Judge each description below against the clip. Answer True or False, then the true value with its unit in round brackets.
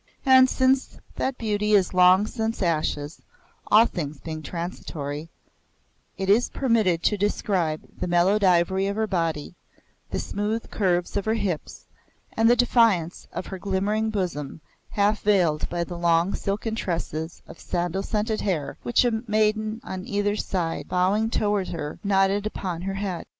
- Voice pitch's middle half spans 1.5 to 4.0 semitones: True (3.7 semitones)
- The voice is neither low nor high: False (195 Hz)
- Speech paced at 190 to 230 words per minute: False (155 wpm)